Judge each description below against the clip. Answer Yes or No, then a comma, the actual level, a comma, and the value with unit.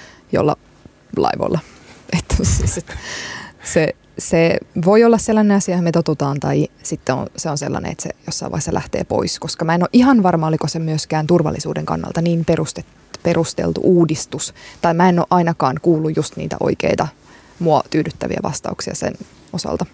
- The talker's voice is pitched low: No, medium, 170 Hz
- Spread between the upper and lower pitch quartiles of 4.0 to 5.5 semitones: No, narrow, 2.4 semitones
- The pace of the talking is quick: Yes, fast, 165 wpm